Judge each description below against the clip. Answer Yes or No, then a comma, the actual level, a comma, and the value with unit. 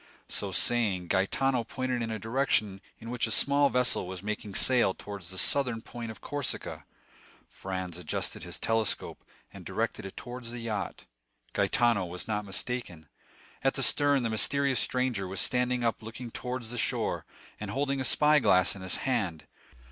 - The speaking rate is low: No, average, 170 wpm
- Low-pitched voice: Yes, low, 115 Hz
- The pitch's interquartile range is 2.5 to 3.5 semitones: No, average, 4.4 semitones